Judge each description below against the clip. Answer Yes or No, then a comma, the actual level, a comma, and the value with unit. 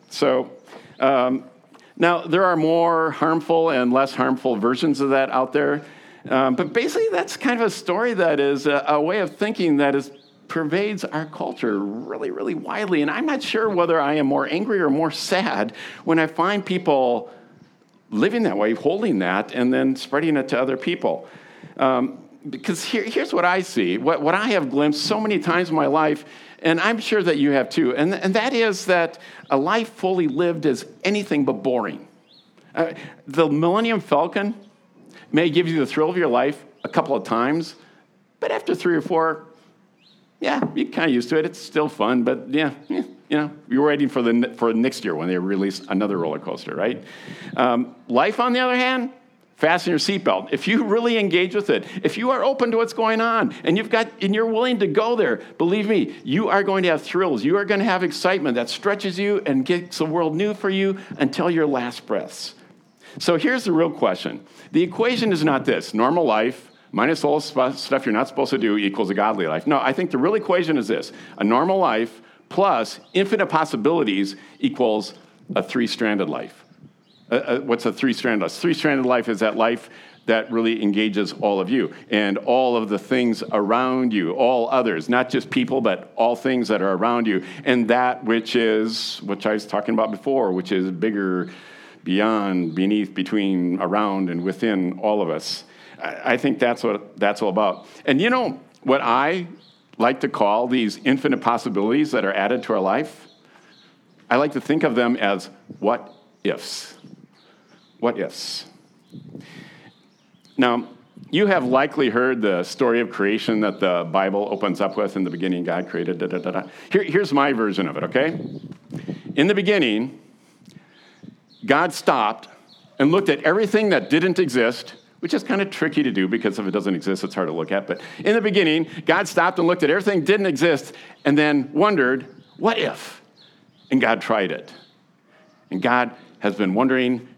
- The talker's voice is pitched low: No, medium, 150 Hz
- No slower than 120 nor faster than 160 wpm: No, average, 190 wpm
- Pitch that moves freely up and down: Yes, wide, 8.1 semitones